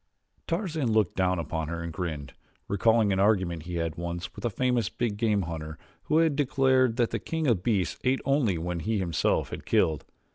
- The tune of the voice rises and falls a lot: Yes, wide, 6.5 semitones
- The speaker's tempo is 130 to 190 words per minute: No, fast, 205 wpm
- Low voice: Yes, low, 100 Hz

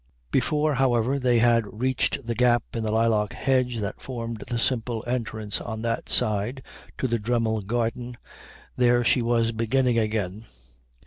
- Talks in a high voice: No, low, 115 Hz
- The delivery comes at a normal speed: Yes, average, 150 wpm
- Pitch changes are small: Yes, narrow, 1.9 semitones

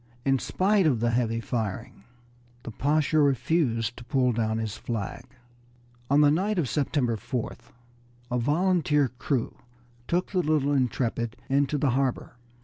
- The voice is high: No, low, 135 Hz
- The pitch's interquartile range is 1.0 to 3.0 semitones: No, average, 4.2 semitones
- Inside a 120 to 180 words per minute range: Yes, average, 140 wpm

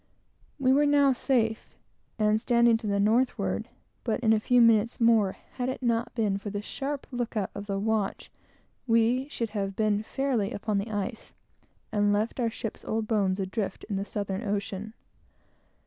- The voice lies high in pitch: Yes, high, 220 Hz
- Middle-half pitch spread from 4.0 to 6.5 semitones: No, average, 2.8 semitones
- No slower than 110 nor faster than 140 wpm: No, average, 175 wpm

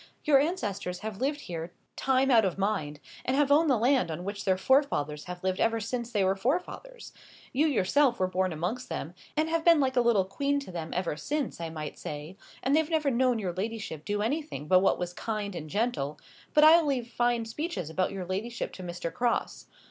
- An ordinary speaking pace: No, fast, 210 wpm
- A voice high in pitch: Yes, high, 220 Hz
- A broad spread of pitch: Yes, wide, 6.9 semitones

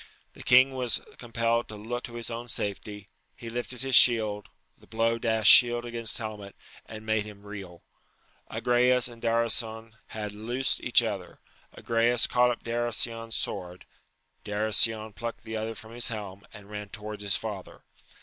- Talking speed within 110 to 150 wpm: No, average, 160 wpm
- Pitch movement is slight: Yes, narrow, 2.1 semitones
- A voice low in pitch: Yes, low, 115 Hz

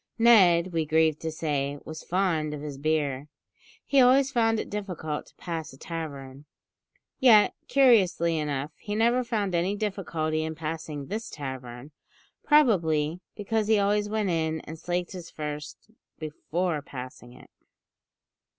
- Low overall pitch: No, medium, 165 Hz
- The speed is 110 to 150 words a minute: Yes, average, 140 wpm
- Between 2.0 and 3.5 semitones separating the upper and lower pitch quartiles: No, wide, 5.5 semitones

